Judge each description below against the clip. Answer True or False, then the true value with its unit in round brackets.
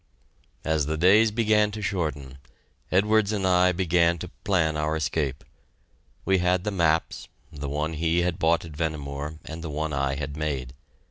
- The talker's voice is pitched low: True (80 Hz)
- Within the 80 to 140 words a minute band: False (170 wpm)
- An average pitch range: True (3.4 semitones)